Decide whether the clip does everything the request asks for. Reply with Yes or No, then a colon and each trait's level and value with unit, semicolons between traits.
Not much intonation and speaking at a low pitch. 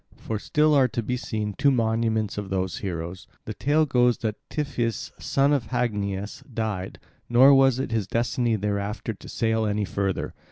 No: average, 3.4 semitones; low, 110 Hz